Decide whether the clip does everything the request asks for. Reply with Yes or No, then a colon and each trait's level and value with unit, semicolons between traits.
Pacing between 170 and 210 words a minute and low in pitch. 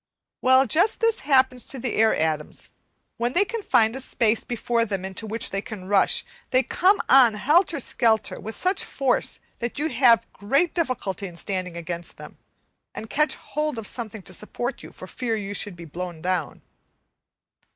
No: average, 175 wpm; high, 230 Hz